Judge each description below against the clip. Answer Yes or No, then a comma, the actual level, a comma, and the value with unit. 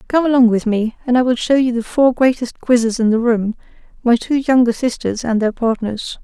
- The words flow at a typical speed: No, fast, 220 wpm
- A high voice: Yes, high, 240 Hz